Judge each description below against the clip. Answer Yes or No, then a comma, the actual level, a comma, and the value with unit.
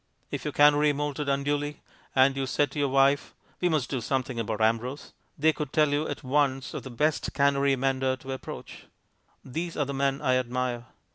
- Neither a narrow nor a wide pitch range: No, narrow, 2.0 semitones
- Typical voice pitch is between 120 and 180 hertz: Yes, medium, 140 Hz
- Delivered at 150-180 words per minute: No, average, 195 wpm